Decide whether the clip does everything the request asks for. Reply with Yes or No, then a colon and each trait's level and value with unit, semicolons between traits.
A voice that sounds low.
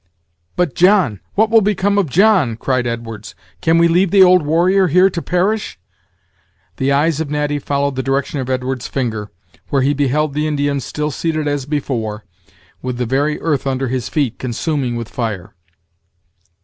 No: medium, 145 Hz